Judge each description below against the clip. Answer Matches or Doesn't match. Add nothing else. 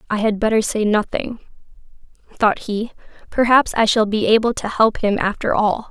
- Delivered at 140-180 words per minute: Matches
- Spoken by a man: Doesn't match